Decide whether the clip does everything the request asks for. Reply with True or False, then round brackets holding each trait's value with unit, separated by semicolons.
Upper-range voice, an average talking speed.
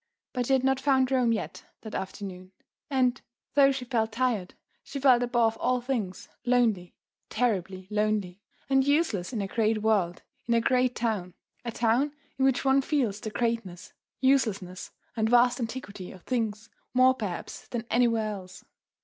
True (230 Hz; 160 wpm)